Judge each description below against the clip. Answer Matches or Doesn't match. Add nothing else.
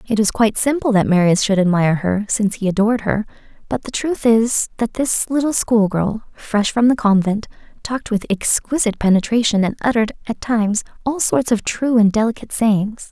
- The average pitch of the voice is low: Doesn't match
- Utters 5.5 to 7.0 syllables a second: Matches